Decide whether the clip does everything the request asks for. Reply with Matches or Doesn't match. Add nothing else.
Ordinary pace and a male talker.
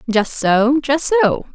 Doesn't match